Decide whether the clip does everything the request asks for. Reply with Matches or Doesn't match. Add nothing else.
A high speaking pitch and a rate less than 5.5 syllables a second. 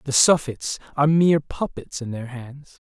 Doesn't match